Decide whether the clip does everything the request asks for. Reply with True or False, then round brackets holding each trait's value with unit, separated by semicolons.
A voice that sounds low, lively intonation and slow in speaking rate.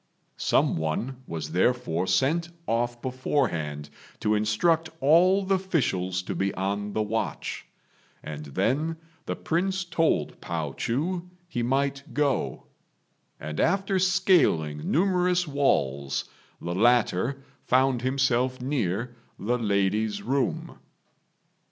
True (125 Hz; 8.6 semitones; 110 wpm)